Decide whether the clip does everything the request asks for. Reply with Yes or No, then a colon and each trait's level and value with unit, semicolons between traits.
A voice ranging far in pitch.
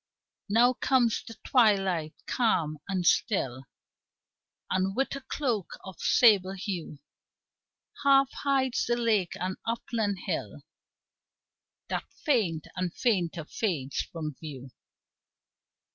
Yes: wide, 6.0 semitones